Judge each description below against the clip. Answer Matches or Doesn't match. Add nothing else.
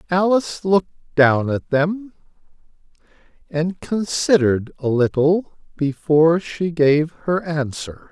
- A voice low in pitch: Doesn't match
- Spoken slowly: Matches